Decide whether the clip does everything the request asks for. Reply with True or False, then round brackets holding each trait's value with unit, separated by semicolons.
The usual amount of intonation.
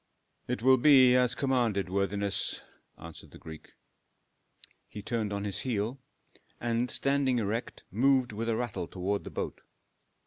True (3.9 semitones)